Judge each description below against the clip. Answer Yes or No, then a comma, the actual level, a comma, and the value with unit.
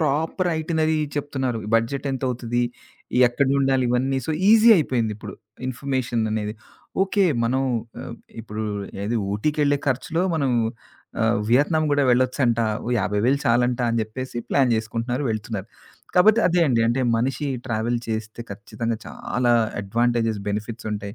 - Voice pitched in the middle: No, low, 125 Hz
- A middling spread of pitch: Yes, average, 3.6 semitones